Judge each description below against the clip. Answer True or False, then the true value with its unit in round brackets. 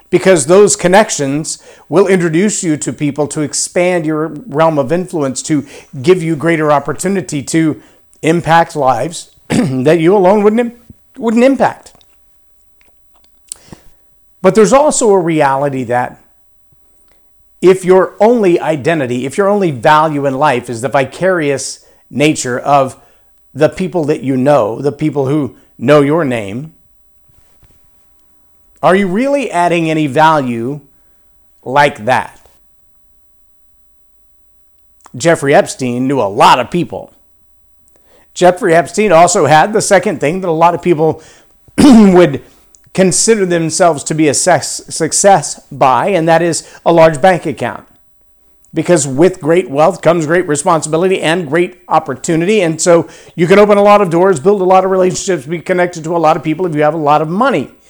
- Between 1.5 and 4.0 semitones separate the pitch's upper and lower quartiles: False (4.6 semitones)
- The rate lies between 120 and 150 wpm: True (145 wpm)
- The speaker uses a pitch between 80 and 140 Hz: False (160 Hz)